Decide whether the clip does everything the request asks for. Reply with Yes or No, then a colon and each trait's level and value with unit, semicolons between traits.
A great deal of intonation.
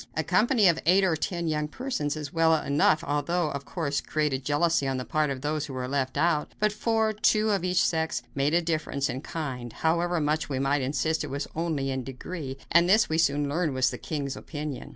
No: average, 3.5 semitones